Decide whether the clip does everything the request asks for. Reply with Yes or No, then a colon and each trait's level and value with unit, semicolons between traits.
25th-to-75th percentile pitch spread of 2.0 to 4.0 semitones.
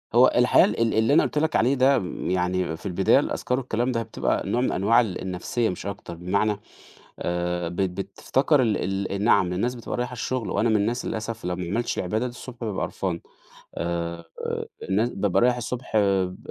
No: average, 4.9 semitones